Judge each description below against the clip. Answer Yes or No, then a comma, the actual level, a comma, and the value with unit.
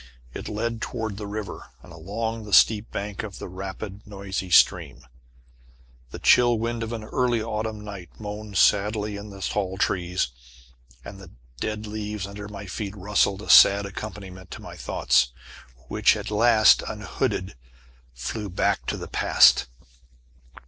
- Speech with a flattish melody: Yes, narrow, 1.9 semitones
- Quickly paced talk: No, average, 150 wpm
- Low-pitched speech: Yes, low, 105 Hz